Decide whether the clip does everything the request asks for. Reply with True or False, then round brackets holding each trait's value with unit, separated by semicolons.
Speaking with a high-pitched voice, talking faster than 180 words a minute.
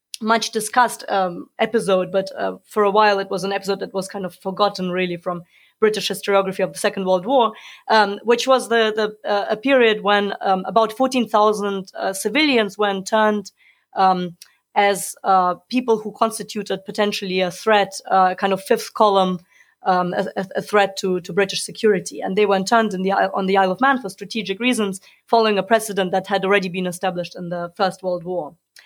True (200 Hz; 195 wpm)